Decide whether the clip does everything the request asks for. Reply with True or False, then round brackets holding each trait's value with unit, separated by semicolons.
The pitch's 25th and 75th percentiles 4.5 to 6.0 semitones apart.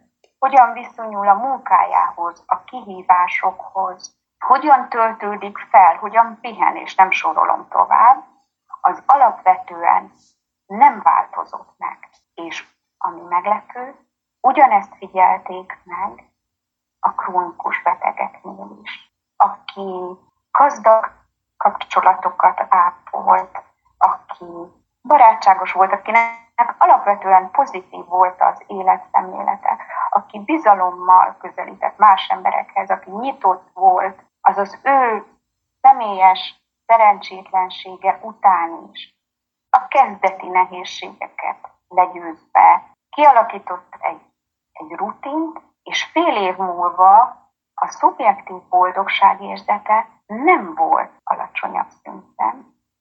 True (5.4 semitones)